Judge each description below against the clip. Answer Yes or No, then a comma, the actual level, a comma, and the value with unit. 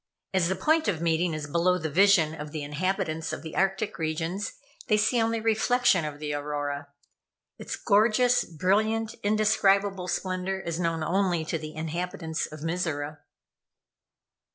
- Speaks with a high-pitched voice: No, medium, 180 Hz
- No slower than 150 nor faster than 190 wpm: Yes, average, 155 wpm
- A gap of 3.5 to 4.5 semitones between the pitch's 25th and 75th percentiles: Yes, average, 4.2 semitones